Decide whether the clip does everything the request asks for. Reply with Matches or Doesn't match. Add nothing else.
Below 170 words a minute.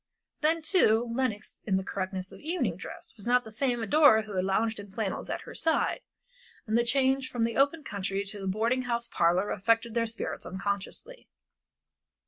Doesn't match